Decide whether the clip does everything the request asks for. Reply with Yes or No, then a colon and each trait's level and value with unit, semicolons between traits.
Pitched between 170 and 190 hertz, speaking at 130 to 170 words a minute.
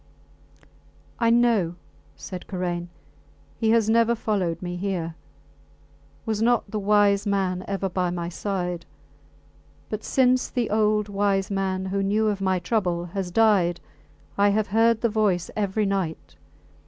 No: high, 200 Hz; average, 140 wpm